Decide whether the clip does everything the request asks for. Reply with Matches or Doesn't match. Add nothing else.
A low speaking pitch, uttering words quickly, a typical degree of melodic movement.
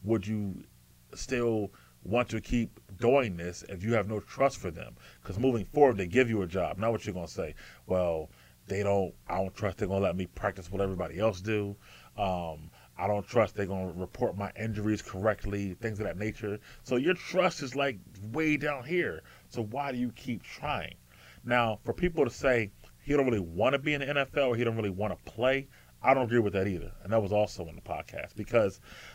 Matches